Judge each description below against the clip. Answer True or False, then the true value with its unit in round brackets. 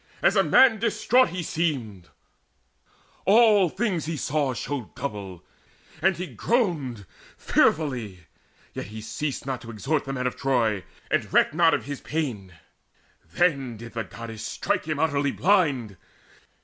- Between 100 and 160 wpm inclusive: True (145 wpm)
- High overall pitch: False (140 Hz)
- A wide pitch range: True (6.5 semitones)